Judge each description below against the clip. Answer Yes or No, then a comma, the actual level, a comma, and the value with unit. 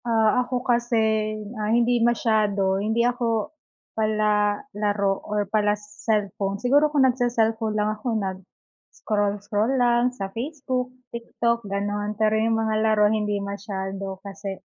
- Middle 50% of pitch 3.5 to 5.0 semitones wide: No, narrow, 2.5 semitones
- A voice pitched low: No, high, 215 Hz